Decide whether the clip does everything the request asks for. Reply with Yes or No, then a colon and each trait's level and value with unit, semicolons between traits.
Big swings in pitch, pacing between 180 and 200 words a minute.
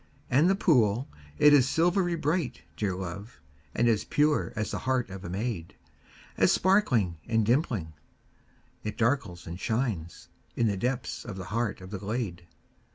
No: wide, 6.0 semitones; average, 160 wpm